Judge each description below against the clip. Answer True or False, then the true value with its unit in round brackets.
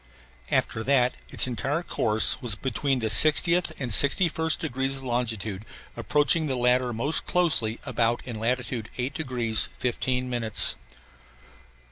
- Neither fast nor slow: False (130 wpm)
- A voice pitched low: True (125 Hz)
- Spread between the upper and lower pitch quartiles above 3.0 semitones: True (3.6 semitones)